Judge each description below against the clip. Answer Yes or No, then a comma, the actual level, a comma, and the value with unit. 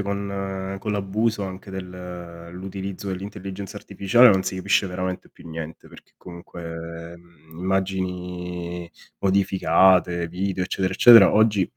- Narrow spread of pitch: Yes, narrow, 1.9 semitones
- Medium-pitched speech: No, very low, 95 Hz